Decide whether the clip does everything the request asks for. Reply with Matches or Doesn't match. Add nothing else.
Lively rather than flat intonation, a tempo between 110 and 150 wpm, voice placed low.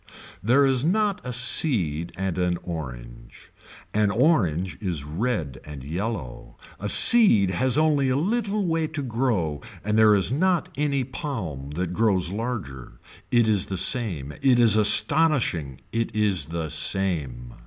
Matches